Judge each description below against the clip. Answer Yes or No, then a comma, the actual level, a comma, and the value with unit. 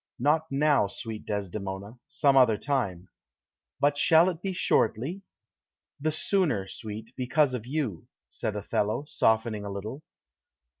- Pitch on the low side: Yes, low, 125 Hz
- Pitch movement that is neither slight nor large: No, wide, 6.1 semitones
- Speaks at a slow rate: Yes, slow, 130 wpm